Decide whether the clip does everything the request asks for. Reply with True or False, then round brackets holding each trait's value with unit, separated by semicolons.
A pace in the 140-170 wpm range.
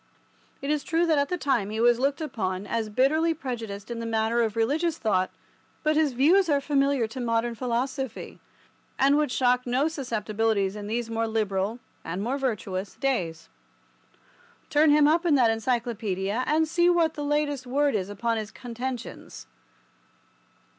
True (165 wpm)